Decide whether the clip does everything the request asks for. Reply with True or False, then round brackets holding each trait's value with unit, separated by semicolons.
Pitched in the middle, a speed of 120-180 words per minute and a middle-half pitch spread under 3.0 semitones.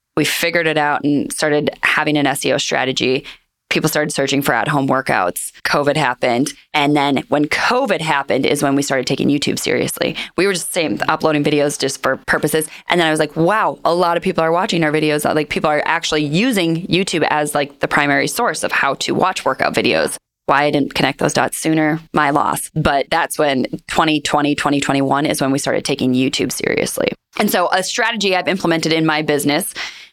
False (150 Hz; 200 wpm; 2.5 semitones)